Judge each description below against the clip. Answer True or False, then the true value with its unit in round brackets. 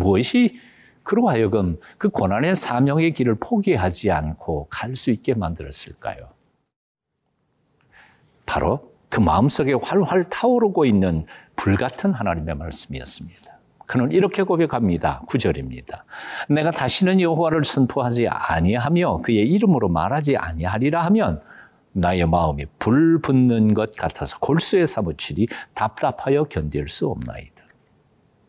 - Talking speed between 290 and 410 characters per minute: True (295 characters per minute)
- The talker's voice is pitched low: True (125 Hz)